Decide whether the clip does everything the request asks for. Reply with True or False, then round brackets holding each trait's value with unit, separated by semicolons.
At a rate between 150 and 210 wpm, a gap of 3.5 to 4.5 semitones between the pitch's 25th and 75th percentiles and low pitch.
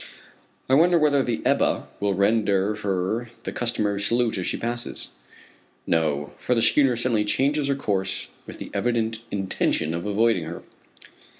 True (155 wpm; 3.9 semitones; 110 Hz)